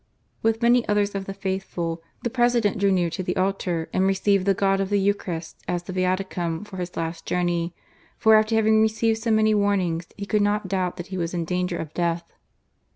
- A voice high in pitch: Yes, high, 195 Hz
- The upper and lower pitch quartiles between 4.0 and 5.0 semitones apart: No, average, 2.9 semitones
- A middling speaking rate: No, fast, 210 wpm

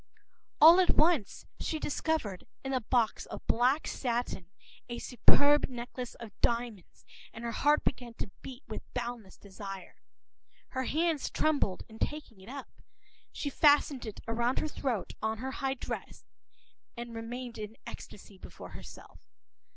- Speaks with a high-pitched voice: Yes, high, 245 Hz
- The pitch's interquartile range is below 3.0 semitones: No, average, 4.0 semitones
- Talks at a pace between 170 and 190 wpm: No, average, 150 wpm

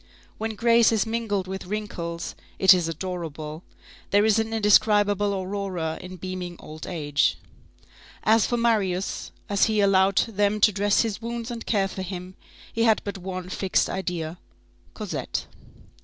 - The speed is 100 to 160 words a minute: Yes, average, 150 wpm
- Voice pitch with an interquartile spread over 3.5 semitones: No, average, 2.9 semitones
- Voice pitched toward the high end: Yes, high, 195 Hz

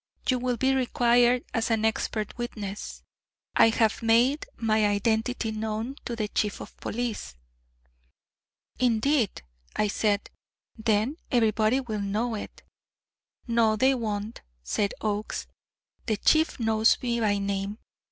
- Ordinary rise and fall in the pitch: No, narrow, 2.2 semitones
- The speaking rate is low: Yes, slow, 125 wpm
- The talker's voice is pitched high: Yes, high, 225 Hz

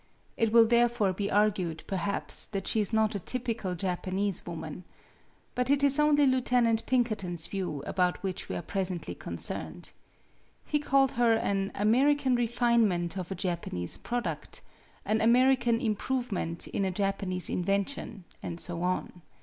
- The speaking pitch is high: Yes, high, 205 Hz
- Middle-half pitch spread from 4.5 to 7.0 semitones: Yes, average, 4.8 semitones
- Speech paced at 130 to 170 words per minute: Yes, average, 150 wpm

